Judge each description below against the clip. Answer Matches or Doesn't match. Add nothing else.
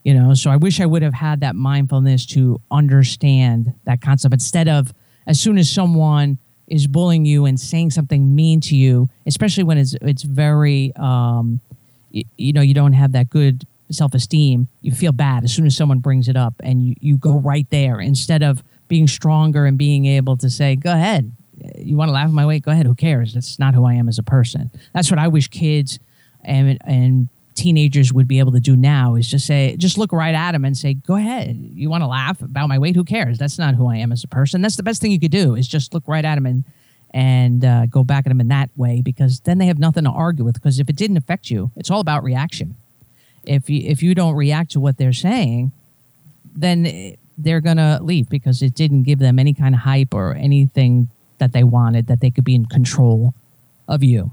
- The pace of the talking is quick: Matches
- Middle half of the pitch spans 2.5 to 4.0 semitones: Matches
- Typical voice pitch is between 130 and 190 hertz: Matches